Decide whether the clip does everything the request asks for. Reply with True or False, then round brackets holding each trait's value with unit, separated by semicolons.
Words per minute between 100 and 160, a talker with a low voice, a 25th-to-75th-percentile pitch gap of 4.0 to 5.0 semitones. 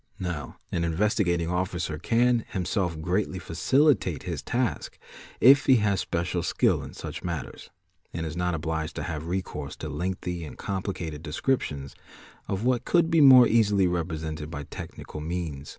True (150 wpm; 90 Hz; 4.7 semitones)